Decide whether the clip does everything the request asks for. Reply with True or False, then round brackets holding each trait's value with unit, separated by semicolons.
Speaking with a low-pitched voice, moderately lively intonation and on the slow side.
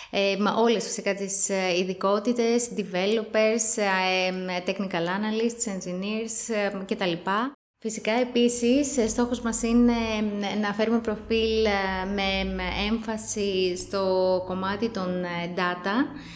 False (205 Hz; 3.1 semitones; 90 wpm)